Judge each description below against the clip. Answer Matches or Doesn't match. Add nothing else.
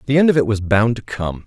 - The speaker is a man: Matches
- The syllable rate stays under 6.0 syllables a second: Doesn't match